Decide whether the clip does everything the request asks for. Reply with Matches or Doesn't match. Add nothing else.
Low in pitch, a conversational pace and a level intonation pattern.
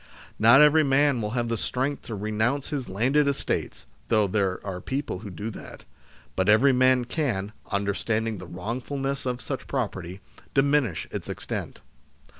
Doesn't match